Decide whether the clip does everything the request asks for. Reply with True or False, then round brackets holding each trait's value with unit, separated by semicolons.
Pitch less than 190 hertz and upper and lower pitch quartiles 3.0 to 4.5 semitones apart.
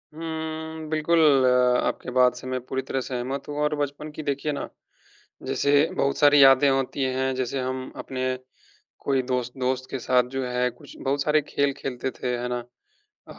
False (135 Hz; 2.4 semitones)